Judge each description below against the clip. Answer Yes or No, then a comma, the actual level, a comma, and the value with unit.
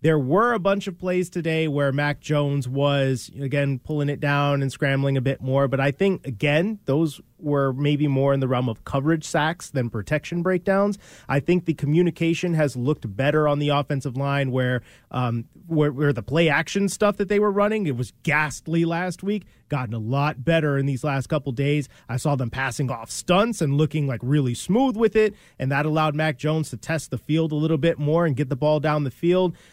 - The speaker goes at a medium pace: No, fast, 215 wpm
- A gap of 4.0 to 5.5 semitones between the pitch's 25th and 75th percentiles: No, average, 3.4 semitones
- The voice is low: No, medium, 150 Hz